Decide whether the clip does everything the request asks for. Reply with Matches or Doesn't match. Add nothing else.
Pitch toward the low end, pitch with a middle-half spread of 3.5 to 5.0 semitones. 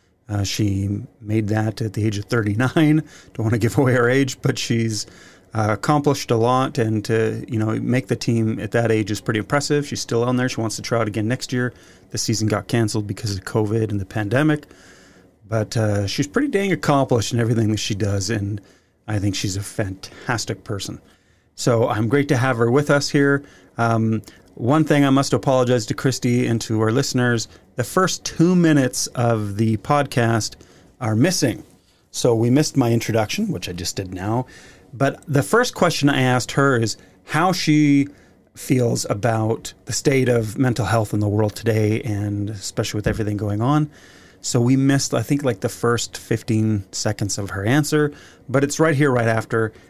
Matches